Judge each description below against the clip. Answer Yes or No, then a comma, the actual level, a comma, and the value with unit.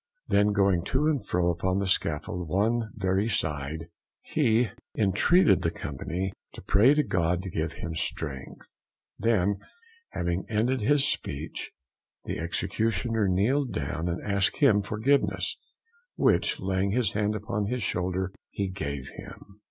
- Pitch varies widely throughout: No, average, 4.2 semitones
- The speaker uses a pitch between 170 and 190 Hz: No, low, 100 Hz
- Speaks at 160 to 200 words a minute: No, average, 140 wpm